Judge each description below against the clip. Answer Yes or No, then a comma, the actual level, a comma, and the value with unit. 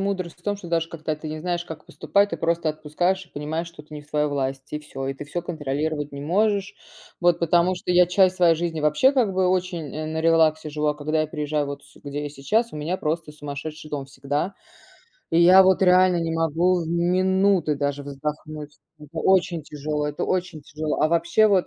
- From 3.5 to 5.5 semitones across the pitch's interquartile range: No, average, 3.1 semitones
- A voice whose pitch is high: No, medium, 160 Hz